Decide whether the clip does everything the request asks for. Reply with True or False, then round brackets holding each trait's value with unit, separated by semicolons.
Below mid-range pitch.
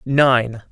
True (125 Hz)